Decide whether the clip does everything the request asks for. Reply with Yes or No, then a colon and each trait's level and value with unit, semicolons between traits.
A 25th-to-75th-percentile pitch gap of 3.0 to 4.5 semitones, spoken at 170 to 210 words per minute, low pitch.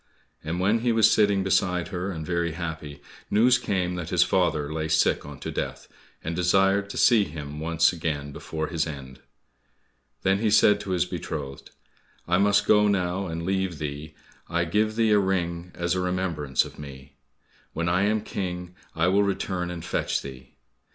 Yes: average, 3.6 semitones; average, 180 wpm; very low, 90 Hz